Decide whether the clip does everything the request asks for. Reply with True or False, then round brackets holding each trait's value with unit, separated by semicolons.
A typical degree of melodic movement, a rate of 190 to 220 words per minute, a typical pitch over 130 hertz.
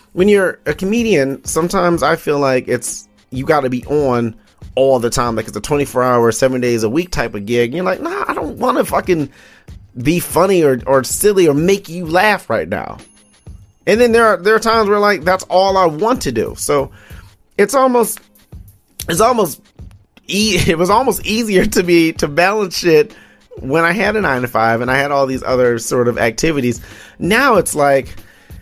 False (7.6 semitones; 205 wpm; 140 Hz)